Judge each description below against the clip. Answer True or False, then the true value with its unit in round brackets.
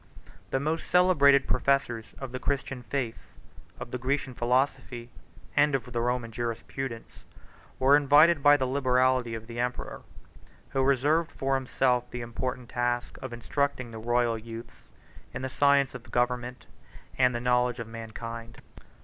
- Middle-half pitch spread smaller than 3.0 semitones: True (2.5 semitones)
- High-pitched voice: False (125 Hz)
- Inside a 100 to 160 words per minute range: True (150 wpm)